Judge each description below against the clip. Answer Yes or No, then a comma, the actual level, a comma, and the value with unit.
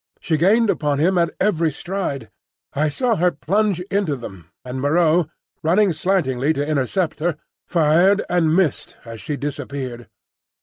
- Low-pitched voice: No, medium, 160 Hz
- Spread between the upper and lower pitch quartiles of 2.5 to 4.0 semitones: No, average, 4.5 semitones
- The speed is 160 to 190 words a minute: No, average, 145 wpm